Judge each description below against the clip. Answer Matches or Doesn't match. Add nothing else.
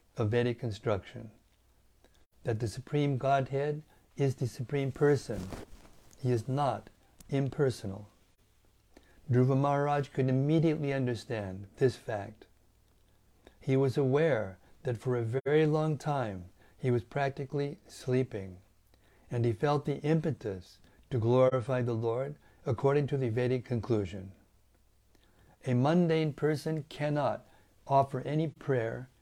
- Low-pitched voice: Matches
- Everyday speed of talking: Doesn't match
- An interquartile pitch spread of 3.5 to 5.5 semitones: Matches